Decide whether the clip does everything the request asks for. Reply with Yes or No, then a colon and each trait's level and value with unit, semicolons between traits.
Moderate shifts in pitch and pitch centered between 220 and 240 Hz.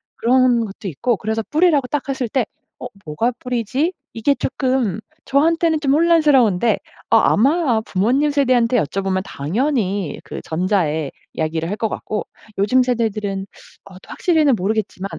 No: wide, 5.7 semitones; high, 230 Hz